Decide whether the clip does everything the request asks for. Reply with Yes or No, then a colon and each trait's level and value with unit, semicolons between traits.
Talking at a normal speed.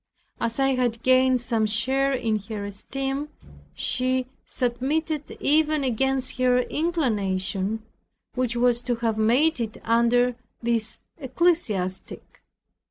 No: slow, 110 wpm